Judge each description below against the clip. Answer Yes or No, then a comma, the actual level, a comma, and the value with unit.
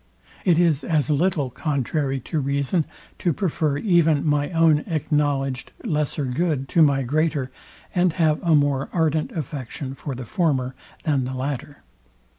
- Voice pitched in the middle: Yes, medium, 150 Hz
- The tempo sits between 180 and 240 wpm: No, average, 145 wpm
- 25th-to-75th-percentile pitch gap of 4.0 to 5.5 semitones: No, average, 3.0 semitones